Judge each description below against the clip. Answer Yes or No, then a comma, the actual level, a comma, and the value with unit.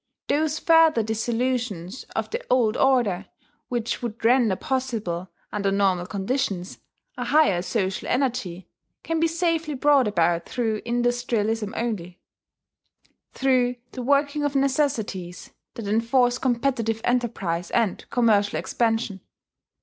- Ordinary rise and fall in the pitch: Yes, average, 4.5 semitones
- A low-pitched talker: No, high, 235 Hz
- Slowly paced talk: Yes, slow, 115 wpm